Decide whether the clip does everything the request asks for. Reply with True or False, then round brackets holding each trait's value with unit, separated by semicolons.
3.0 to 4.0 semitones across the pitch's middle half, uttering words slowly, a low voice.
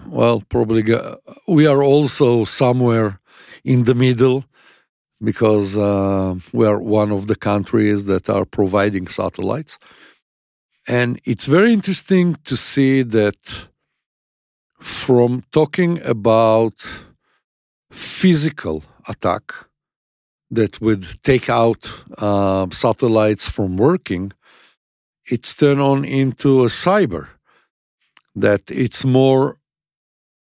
False (4.8 semitones; 100 wpm; 115 Hz)